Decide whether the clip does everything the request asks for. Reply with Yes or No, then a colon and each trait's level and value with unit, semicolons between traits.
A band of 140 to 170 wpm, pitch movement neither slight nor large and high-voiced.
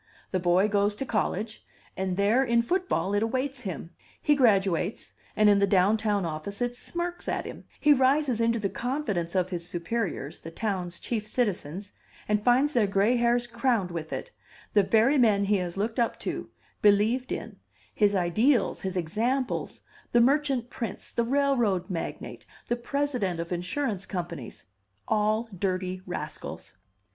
Yes: average, 160 wpm; average, 4.7 semitones; high, 210 Hz